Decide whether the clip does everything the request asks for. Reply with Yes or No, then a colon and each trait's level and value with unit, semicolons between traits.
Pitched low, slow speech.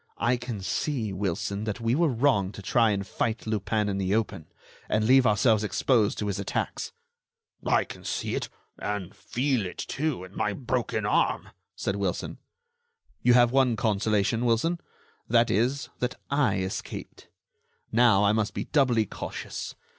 No: low, 110 Hz; average, 160 wpm